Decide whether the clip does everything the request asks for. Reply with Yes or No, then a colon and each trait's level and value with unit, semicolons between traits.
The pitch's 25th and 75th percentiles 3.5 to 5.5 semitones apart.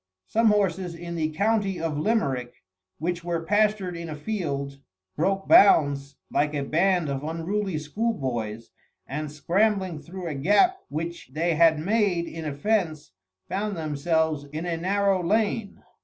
Yes: average, 4.7 semitones